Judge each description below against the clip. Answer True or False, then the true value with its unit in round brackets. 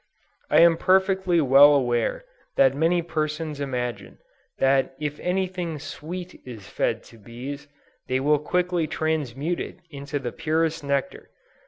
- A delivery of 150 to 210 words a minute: False (140 wpm)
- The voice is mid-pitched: True (150 Hz)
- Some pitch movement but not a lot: True (4.1 semitones)